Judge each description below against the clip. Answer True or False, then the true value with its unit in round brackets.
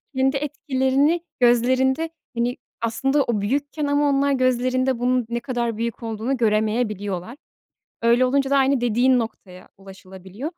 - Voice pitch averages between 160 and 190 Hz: False (250 Hz)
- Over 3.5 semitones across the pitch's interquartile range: False (3.0 semitones)